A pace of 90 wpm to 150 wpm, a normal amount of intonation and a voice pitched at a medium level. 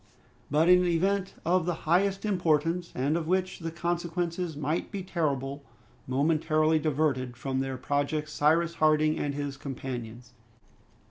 Yes: slow, 135 wpm; average, 3.4 semitones; medium, 155 Hz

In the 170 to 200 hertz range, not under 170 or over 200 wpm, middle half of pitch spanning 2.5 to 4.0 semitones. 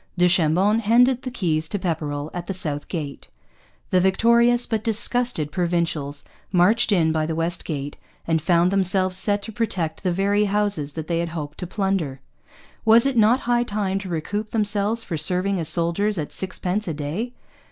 No: medium, 185 Hz; average, 180 wpm; average, 4.5 semitones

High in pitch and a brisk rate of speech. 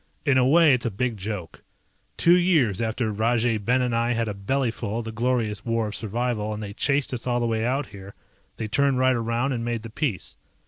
No: low, 115 Hz; fast, 225 wpm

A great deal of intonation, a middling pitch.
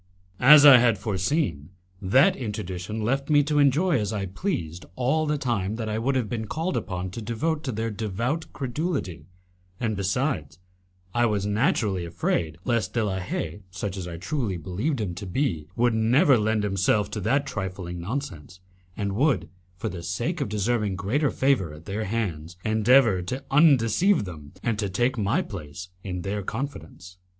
No: wide, 6.1 semitones; low, 110 Hz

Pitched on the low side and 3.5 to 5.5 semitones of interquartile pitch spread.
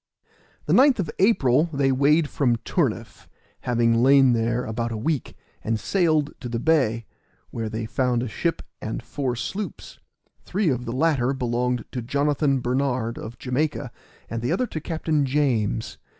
Yes: low, 130 Hz; average, 4.1 semitones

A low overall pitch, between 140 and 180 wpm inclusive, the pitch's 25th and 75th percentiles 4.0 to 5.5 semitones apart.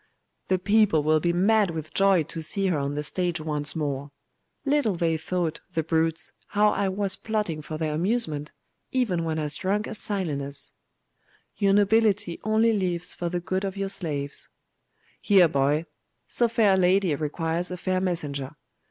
No: medium, 175 Hz; average, 170 wpm; average, 4.3 semitones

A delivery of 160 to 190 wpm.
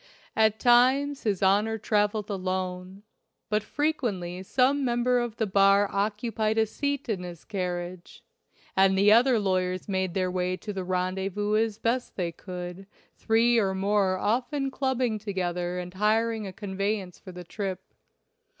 No: average, 150 wpm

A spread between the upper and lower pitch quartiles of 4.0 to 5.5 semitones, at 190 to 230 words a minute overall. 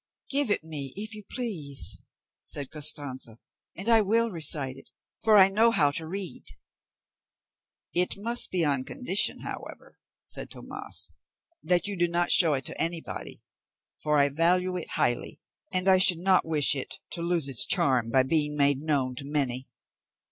No: average, 5.2 semitones; average, 165 wpm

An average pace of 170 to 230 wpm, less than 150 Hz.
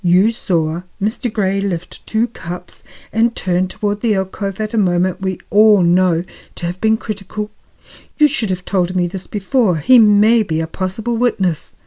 No: average, 175 wpm; high, 195 Hz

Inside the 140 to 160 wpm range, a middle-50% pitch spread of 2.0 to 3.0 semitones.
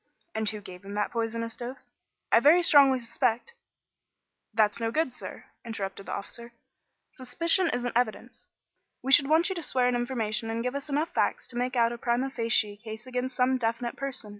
No: average, 190 wpm; narrow, 2.6 semitones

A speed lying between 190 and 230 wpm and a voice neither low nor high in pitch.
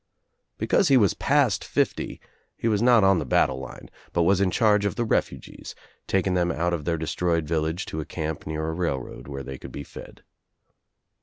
No: average, 200 wpm; very low, 85 Hz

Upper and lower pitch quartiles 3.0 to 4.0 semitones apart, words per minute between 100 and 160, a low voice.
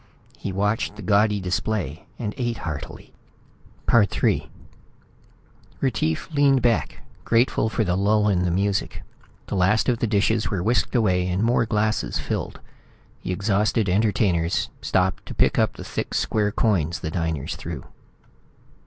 Yes: average, 3.5 semitones; average, 145 wpm; low, 105 Hz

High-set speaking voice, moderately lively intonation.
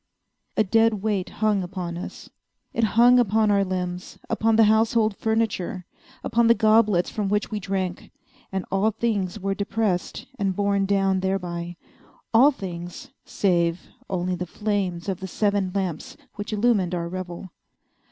Yes: high, 195 Hz; average, 3.0 semitones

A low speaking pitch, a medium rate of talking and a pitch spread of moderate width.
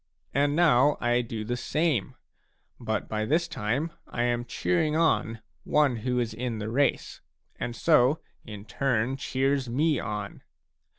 Yes: low, 125 Hz; average, 145 wpm; average, 4.4 semitones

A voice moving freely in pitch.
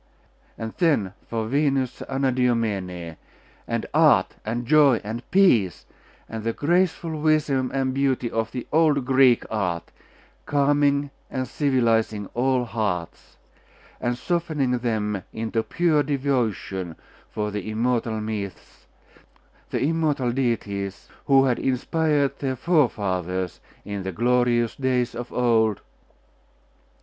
No: average, 4.2 semitones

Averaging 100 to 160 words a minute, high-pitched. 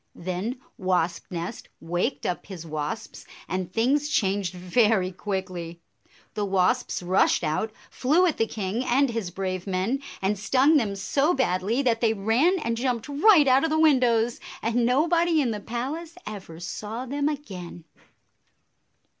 Yes: average, 150 wpm; high, 225 Hz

